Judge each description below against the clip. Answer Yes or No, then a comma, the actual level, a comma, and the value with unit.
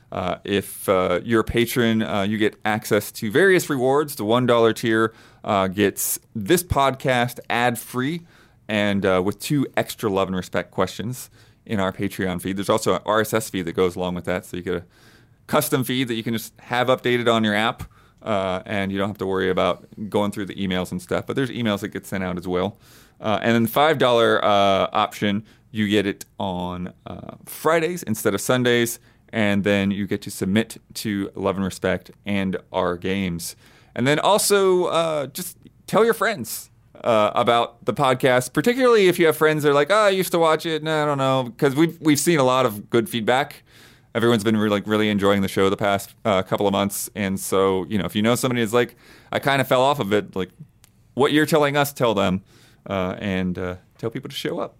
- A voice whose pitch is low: Yes, low, 115 Hz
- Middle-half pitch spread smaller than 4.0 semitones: No, average, 4.4 semitones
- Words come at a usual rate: No, fast, 215 wpm